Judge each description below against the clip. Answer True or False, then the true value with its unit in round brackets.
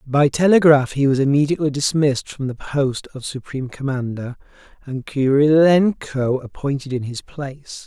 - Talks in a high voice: False (140 Hz)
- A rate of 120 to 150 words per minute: True (135 wpm)